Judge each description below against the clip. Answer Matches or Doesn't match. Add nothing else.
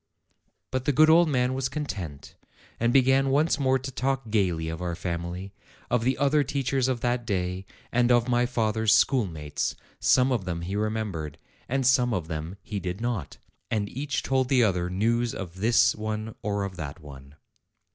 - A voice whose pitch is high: Doesn't match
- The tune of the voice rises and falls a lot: Matches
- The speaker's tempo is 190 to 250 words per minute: Doesn't match